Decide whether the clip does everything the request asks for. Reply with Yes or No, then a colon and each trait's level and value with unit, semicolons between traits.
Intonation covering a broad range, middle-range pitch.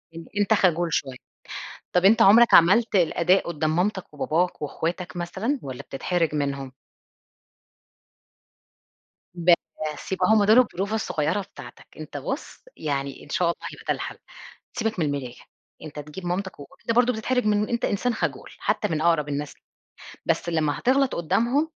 Yes: wide, 5.7 semitones; medium, 175 Hz